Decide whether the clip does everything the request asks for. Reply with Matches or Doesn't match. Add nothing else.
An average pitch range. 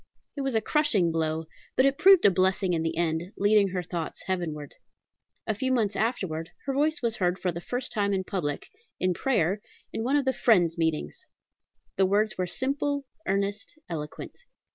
Doesn't match